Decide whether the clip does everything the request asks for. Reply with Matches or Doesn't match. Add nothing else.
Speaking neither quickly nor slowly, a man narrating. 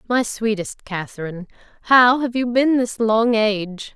Doesn't match